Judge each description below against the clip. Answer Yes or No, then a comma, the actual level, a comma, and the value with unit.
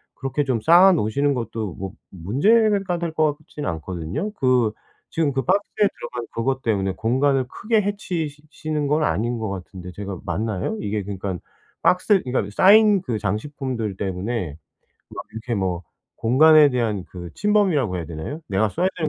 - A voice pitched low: Yes, low, 125 Hz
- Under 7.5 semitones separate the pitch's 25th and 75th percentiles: No, wide, 7.8 semitones